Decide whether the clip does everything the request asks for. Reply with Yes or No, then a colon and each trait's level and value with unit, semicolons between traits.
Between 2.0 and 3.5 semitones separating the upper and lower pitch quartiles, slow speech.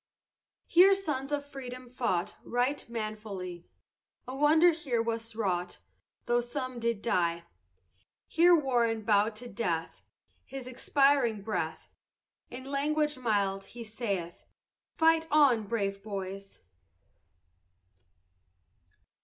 No: average, 5.2 semitones; slow, 105 wpm